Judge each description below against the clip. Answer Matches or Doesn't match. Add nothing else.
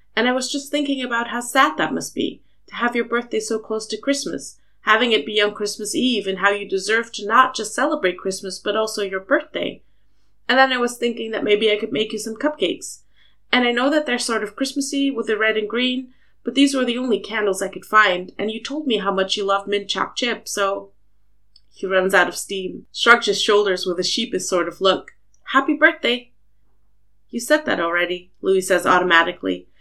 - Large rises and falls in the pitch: Doesn't match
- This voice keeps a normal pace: Doesn't match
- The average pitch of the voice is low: Doesn't match